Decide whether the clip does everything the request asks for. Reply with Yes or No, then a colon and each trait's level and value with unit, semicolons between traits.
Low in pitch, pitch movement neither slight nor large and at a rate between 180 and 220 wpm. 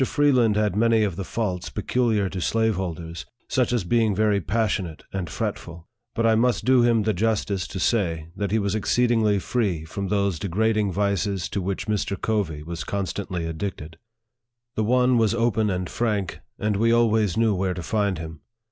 Yes: low, 105 Hz; average, 3.6 semitones; average, 185 wpm